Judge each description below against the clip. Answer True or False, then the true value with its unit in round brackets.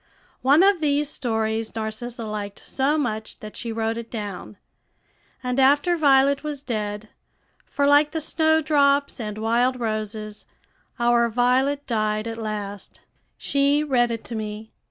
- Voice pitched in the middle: False (240 Hz)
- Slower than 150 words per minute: True (140 wpm)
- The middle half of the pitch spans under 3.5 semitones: False (4.5 semitones)